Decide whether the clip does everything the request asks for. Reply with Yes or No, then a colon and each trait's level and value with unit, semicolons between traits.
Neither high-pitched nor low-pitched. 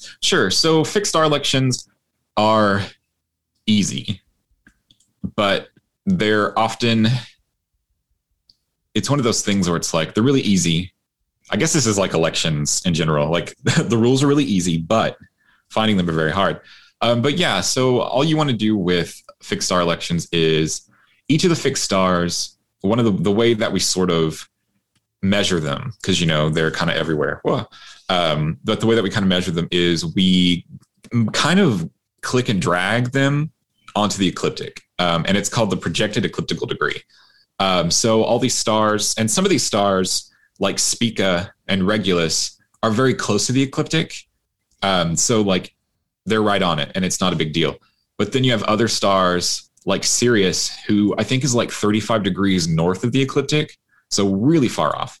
No: low, 105 Hz